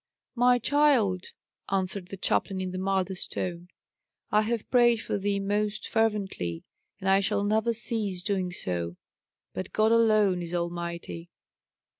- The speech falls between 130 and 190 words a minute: Yes, average, 140 wpm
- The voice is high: Yes, high, 195 Hz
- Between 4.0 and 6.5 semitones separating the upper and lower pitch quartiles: No, average, 3.4 semitones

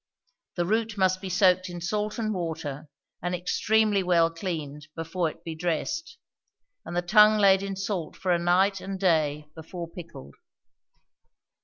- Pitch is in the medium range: Yes, medium, 180 Hz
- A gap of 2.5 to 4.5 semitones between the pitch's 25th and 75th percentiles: Yes, average, 3.1 semitones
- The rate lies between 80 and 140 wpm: No, average, 155 wpm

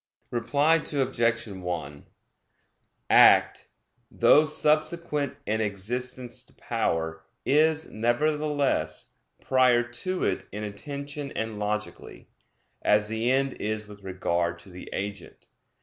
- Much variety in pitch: Yes, wide, 5.9 semitones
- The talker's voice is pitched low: Yes, low, 115 Hz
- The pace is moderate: No, slow, 105 wpm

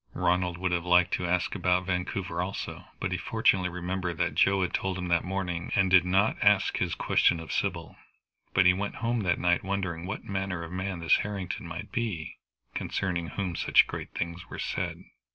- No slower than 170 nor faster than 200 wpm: Yes, average, 195 wpm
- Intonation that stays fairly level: Yes, narrow, 1.6 semitones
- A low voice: Yes, very low, 90 Hz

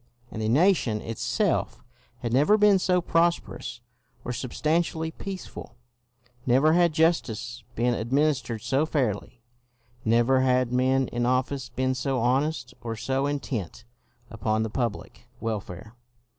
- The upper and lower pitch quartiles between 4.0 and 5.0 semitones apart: Yes, average, 4.6 semitones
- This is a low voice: Yes, low, 130 Hz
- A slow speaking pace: Yes, slow, 130 wpm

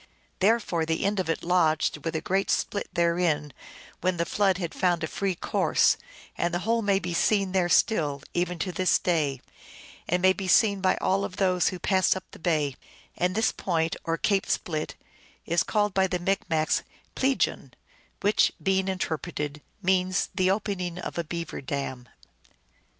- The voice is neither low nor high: Yes, medium, 180 Hz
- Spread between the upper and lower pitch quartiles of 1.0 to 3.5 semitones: Yes, average, 2.8 semitones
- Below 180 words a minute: Yes, average, 170 wpm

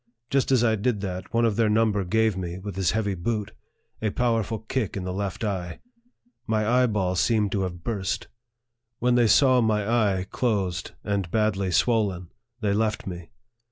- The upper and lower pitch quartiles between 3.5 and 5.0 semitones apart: No, average, 3.1 semitones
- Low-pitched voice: Yes, low, 105 Hz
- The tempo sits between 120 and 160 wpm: No, average, 180 wpm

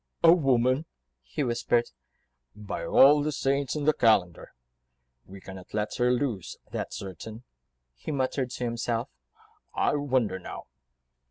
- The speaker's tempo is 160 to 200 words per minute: No, slow, 135 wpm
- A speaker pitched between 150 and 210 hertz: No, low, 120 Hz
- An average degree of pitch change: Yes, average, 4.7 semitones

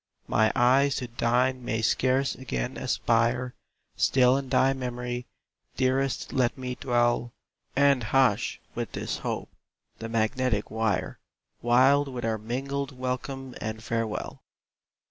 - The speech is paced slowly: Yes, slow, 125 wpm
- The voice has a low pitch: Yes, low, 125 Hz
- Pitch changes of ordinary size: No, narrow, 2.2 semitones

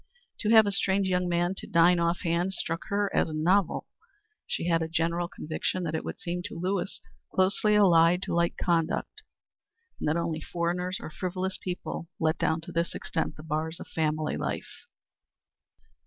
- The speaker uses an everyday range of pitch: No, narrow, 2.2 semitones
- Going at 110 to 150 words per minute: No, average, 175 wpm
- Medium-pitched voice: Yes, medium, 170 Hz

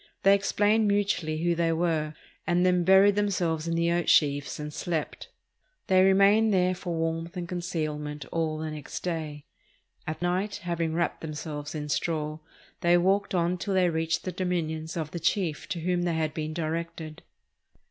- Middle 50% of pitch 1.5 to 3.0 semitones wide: Yes, narrow, 2.6 semitones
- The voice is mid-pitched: Yes, medium, 170 Hz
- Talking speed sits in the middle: Yes, average, 170 wpm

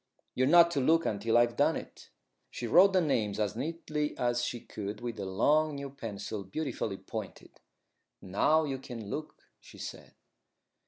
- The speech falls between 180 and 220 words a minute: No, average, 165 wpm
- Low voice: Yes, low, 125 Hz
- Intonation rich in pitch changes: Yes, wide, 6.1 semitones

